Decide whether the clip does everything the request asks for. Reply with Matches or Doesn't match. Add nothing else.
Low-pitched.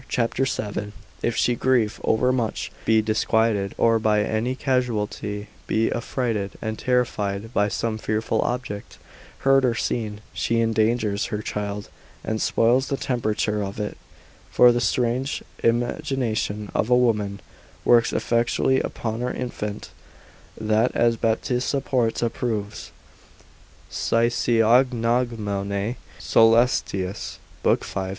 Matches